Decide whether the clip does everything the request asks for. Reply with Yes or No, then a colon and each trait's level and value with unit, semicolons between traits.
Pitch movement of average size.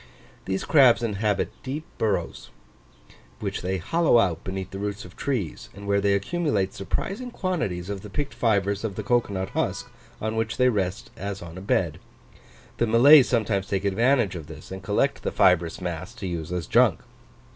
Yes: average, 4.0 semitones